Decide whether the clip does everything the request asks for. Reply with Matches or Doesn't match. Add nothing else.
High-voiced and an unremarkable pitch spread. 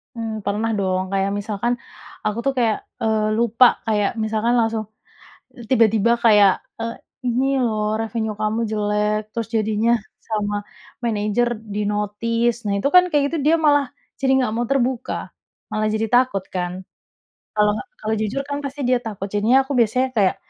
Doesn't match